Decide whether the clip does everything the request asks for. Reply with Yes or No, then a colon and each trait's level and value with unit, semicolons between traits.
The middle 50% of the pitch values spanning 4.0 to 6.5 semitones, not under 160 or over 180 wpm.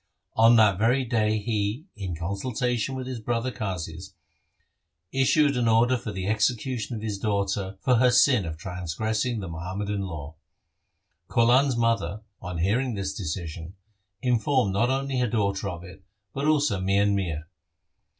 No: average, 4.3 semitones; average, 150 wpm